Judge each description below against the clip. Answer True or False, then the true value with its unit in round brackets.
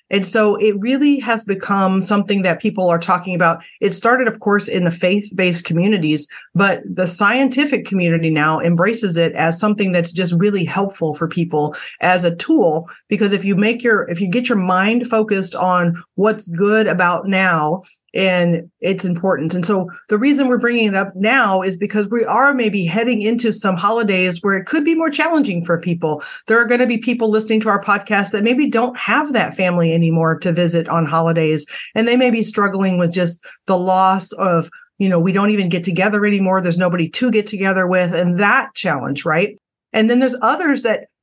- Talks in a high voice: True (195 Hz)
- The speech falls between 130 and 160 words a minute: False (200 wpm)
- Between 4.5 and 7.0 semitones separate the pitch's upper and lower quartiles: False (3.9 semitones)